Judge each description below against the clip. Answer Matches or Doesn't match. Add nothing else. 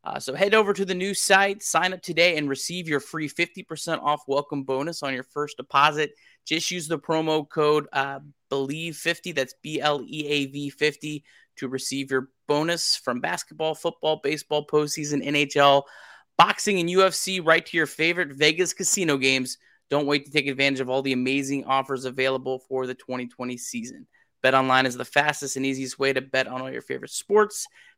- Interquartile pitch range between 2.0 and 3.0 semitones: Doesn't match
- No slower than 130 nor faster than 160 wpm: Doesn't match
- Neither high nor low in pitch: Matches